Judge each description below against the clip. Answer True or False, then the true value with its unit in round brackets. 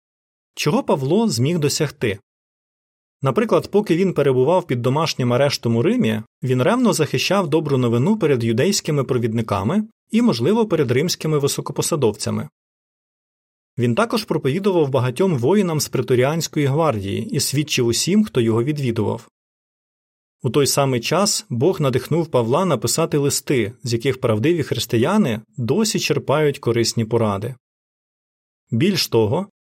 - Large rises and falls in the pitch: True (6.0 semitones)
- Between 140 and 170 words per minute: False (120 wpm)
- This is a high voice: False (140 Hz)